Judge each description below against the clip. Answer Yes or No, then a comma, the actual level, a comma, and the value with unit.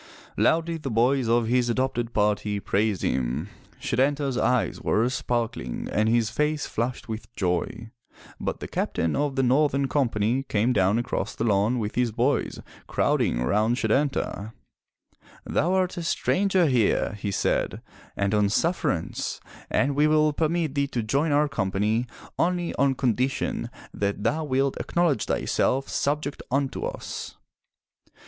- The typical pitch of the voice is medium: No, low, 125 Hz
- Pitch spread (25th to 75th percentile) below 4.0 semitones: No, average, 5.0 semitones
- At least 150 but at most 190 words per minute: No, average, 140 wpm